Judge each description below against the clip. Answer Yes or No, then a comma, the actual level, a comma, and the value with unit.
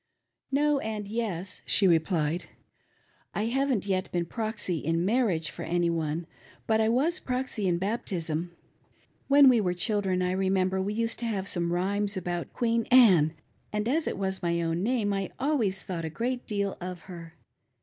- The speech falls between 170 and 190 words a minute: Yes, average, 175 wpm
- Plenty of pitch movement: No, average, 4.7 semitones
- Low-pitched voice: No, high, 195 Hz